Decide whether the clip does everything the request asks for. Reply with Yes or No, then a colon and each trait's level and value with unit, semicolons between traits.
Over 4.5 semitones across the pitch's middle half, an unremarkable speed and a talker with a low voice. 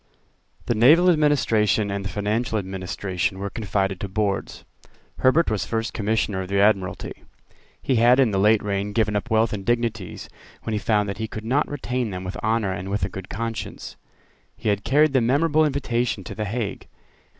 No: average, 3.3 semitones; average, 185 wpm; low, 110 Hz